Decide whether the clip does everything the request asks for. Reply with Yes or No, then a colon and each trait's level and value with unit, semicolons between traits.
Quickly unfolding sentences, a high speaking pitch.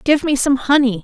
Yes: fast, 235 wpm; very high, 265 Hz